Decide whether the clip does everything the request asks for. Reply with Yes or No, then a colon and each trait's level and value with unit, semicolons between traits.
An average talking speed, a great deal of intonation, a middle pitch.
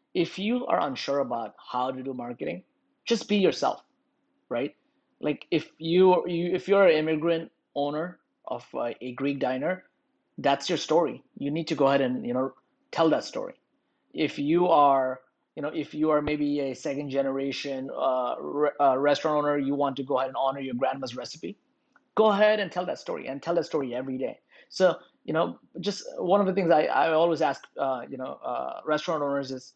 No: average, 195 wpm; average, 4.2 semitones; medium, 150 Hz